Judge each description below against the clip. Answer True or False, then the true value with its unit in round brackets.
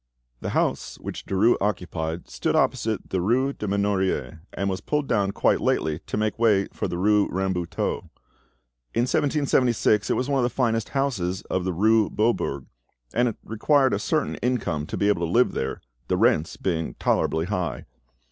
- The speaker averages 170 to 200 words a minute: True (175 wpm)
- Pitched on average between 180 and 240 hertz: False (105 Hz)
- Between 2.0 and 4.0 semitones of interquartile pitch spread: False (4.9 semitones)